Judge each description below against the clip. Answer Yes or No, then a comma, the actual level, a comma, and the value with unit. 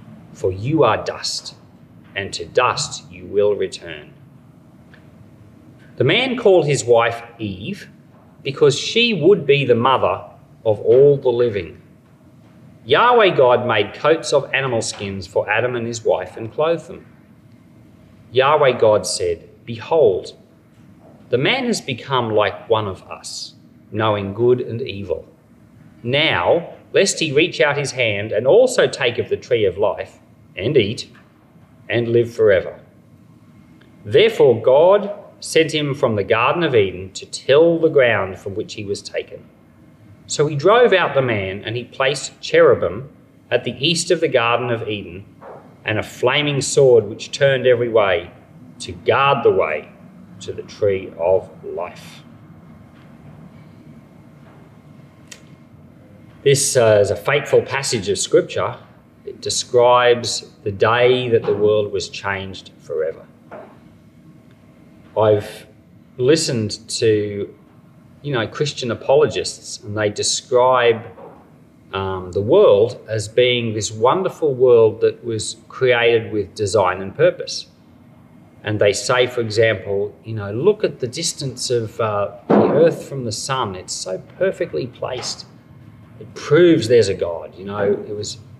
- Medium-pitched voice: No, low, 130 Hz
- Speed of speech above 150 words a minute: No, slow, 135 wpm